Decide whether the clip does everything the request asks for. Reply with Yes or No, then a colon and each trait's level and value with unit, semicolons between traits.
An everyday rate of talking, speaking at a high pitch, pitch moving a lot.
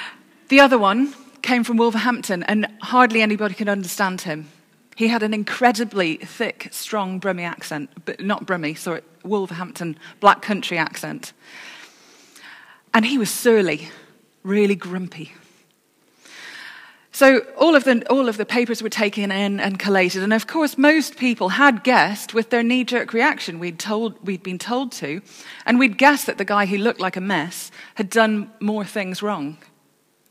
No: average, 160 wpm; high, 210 Hz; average, 4.3 semitones